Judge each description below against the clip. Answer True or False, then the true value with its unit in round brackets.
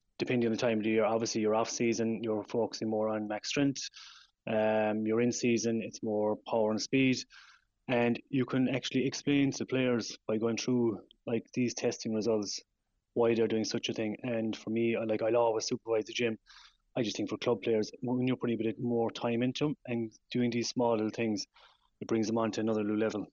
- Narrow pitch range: True (1.6 semitones)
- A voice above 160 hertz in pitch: False (115 Hz)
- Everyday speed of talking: False (210 wpm)